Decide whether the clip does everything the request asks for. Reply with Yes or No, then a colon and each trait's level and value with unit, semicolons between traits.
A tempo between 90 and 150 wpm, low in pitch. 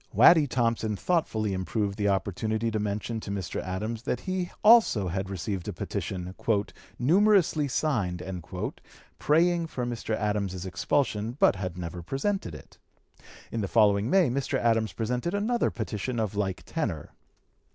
Yes: average, 140 wpm; low, 110 Hz